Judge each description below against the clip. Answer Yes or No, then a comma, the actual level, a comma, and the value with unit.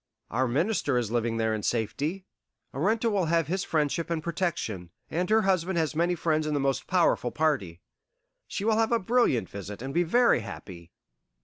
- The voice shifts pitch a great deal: Yes, wide, 7.6 semitones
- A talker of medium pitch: Yes, medium, 155 Hz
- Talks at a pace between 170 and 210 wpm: Yes, average, 185 wpm